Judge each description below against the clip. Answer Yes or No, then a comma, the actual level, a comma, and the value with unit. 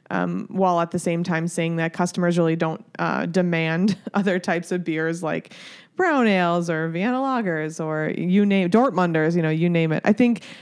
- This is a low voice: No, medium, 175 Hz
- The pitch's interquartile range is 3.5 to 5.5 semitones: No, average, 3.1 semitones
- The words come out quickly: No, average, 190 wpm